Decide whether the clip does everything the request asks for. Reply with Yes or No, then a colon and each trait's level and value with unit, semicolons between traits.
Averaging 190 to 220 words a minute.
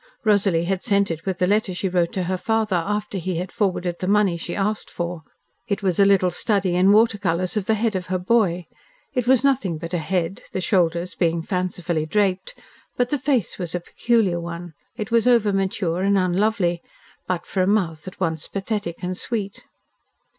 Yes: average, 200 wpm